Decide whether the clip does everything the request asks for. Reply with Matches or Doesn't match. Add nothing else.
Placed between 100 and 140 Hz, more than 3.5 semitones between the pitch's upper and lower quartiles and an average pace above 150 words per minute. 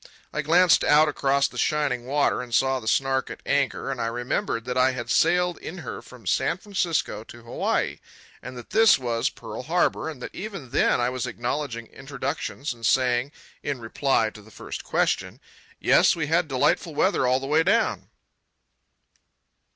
Matches